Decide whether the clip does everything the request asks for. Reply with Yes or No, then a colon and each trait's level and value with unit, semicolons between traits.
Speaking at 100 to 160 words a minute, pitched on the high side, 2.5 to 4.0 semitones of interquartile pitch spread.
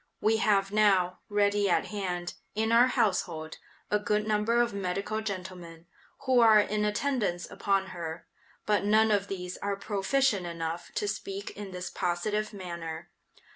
Yes: average, 150 wpm; high, 200 Hz; average, 2.9 semitones